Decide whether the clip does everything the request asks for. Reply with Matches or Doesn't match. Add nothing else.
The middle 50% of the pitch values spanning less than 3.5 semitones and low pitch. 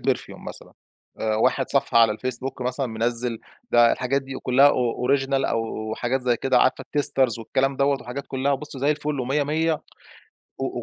Matches